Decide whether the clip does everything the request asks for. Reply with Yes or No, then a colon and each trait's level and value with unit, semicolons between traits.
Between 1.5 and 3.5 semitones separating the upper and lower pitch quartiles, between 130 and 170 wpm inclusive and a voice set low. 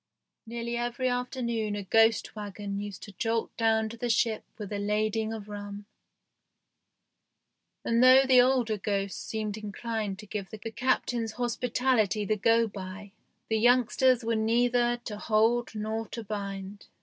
No: narrow, 2.4 semitones; average, 150 wpm; high, 220 Hz